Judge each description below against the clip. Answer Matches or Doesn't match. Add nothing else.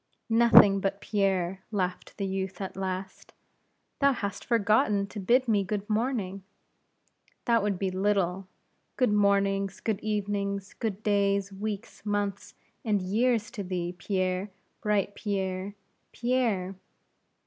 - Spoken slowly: Matches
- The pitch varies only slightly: Matches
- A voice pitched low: Doesn't match